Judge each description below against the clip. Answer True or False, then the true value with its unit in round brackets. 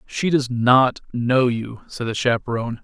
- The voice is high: False (125 Hz)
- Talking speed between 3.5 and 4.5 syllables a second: True (4.4 syllables/s)